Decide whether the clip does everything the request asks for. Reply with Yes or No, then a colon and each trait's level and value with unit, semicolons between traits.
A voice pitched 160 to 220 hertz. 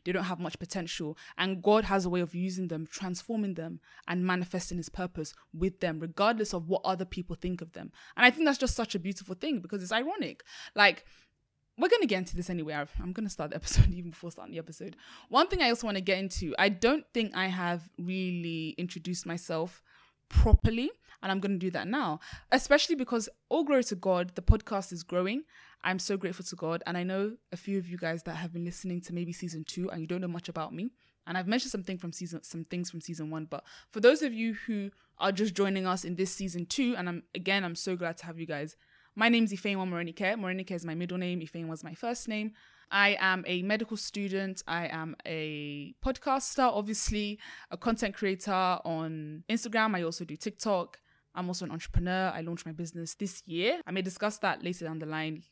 Yes: medium, 185 Hz